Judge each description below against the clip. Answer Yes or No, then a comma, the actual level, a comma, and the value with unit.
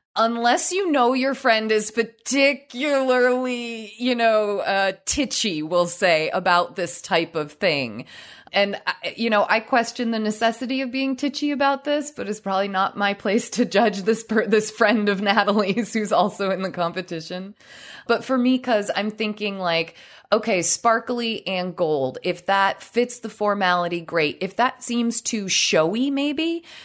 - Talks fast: No, average, 160 wpm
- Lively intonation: No, average, 4.1 semitones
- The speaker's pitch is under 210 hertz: No, high, 220 Hz